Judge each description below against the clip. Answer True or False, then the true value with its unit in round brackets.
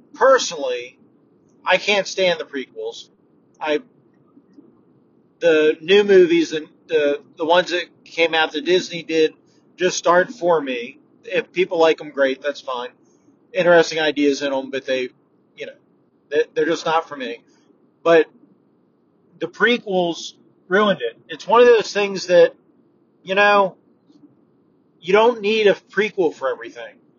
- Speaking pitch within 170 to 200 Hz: True (190 Hz)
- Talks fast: False (140 wpm)